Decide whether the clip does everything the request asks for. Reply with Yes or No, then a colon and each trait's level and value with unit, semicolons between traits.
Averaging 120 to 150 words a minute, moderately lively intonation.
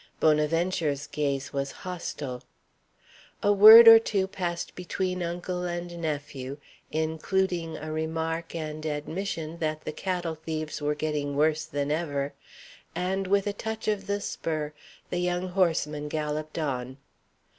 Yes: slow, 135 wpm; average, 3.2 semitones